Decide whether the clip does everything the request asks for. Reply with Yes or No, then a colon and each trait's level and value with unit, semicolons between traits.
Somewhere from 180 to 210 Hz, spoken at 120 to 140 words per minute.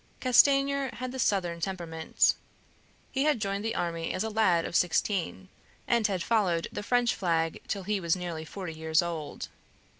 No: high, 190 Hz; average, 170 wpm